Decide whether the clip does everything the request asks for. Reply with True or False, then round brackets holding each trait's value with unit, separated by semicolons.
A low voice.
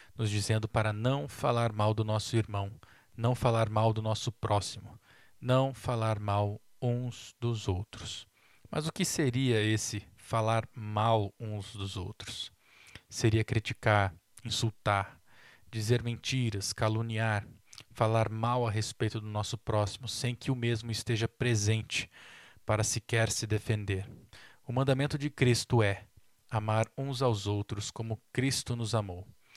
True (110 Hz)